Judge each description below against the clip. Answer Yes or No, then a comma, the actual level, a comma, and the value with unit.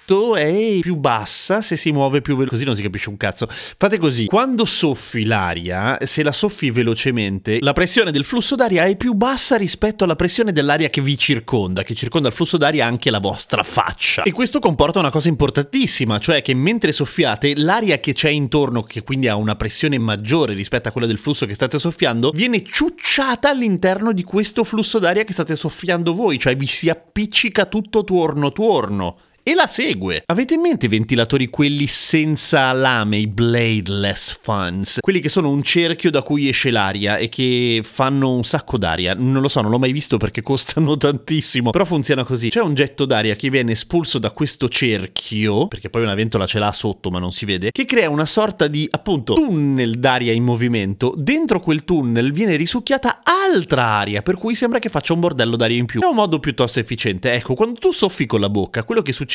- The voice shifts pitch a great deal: Yes, wide, 7.5 semitones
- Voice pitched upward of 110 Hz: Yes, medium, 140 Hz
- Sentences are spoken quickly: Yes, fast, 200 wpm